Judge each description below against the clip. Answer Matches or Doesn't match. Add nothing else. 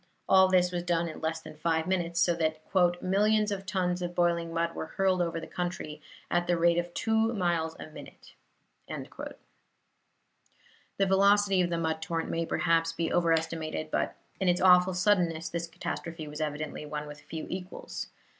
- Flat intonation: Matches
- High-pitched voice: Doesn't match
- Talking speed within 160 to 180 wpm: Matches